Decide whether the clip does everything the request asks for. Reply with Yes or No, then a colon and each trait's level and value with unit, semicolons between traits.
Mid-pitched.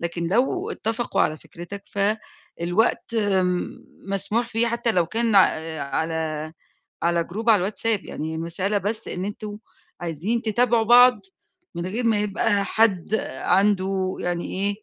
No: high, 200 Hz